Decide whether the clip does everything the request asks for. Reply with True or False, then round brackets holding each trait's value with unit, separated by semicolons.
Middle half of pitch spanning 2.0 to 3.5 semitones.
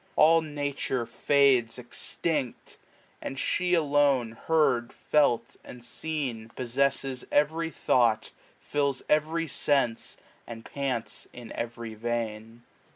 False (3.9 semitones)